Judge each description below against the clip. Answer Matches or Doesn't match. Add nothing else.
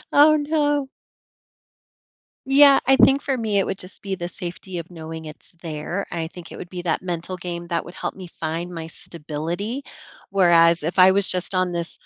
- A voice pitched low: Doesn't match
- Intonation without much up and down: Doesn't match